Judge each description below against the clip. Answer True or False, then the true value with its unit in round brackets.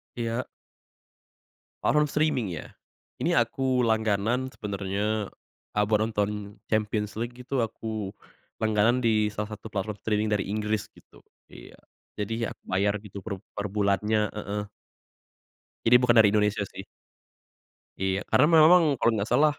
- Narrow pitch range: True (2.1 semitones)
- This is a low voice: True (105 Hz)